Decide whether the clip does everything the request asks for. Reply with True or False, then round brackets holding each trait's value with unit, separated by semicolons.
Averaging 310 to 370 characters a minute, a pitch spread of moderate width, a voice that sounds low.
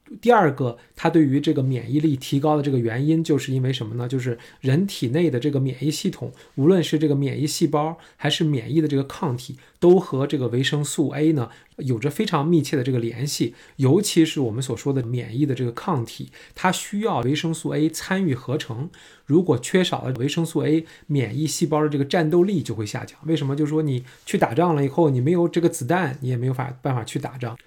False (335 characters per minute; 3.7 semitones; 150 Hz)